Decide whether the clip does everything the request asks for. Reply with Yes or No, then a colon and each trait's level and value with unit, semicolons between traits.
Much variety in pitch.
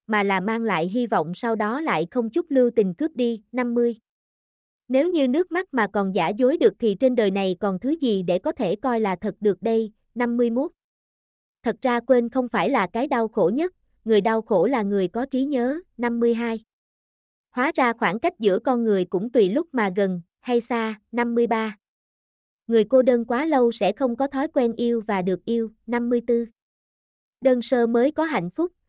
No: average, 3.7 semitones